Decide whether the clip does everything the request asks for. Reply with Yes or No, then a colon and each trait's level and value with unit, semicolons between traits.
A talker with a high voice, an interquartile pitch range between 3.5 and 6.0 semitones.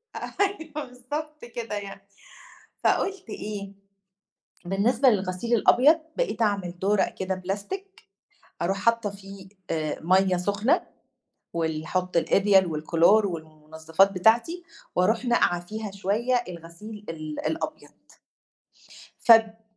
Yes: high, 200 Hz; average, 4.6 semitones